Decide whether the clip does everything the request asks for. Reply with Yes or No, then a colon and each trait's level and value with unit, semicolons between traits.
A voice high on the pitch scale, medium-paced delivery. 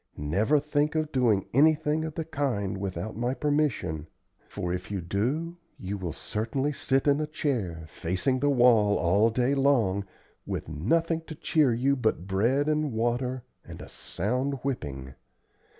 No: low, 125 Hz; average, 155 wpm